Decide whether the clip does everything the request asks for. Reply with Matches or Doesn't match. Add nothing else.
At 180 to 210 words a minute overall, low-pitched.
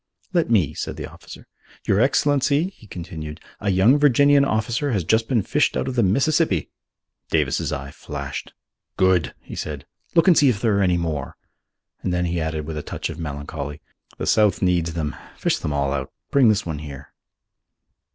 Matches